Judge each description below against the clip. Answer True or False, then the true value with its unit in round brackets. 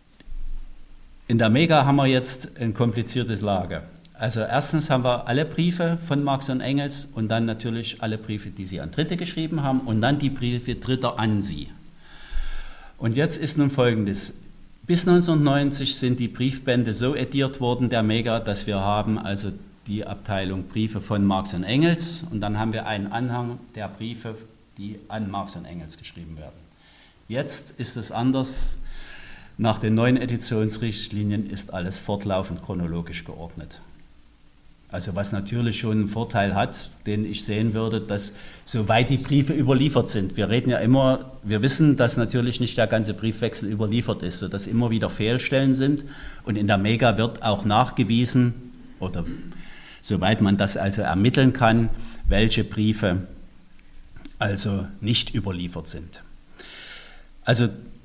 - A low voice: True (115 Hz)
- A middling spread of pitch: True (4.0 semitones)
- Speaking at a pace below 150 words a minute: False (155 wpm)